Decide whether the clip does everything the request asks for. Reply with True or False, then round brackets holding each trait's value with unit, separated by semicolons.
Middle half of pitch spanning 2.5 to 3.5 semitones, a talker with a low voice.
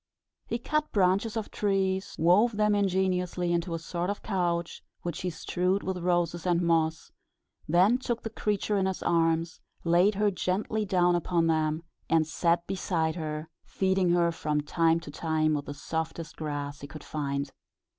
False (2.8 semitones; 175 Hz)